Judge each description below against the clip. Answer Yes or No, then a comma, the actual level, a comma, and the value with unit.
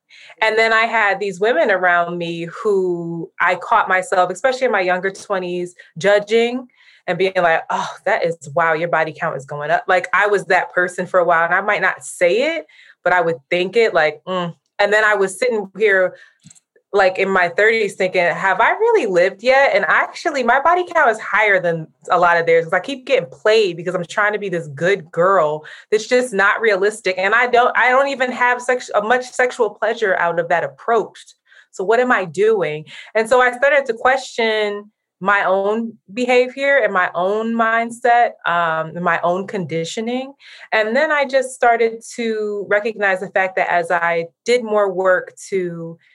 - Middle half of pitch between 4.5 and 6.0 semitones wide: Yes, average, 4.8 semitones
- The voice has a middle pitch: No, high, 200 Hz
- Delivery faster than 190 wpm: Yes, average, 200 wpm